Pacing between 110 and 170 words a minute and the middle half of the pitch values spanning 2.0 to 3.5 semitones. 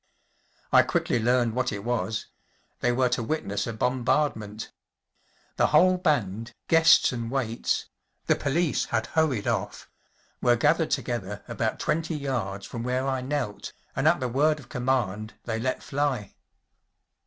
No: average, 140 wpm; average, 4.3 semitones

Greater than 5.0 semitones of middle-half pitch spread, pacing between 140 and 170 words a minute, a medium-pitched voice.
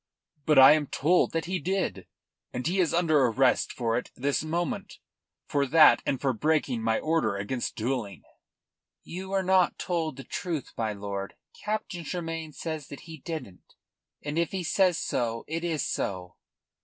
Yes: wide, 5.5 semitones; average, 165 wpm; medium, 155 Hz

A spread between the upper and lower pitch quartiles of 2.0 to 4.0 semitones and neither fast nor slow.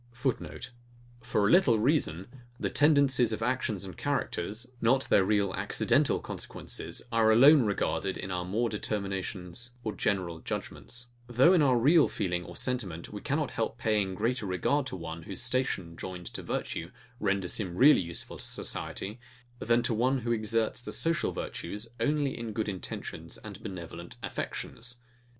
No: average, 4.9 semitones; average, 160 wpm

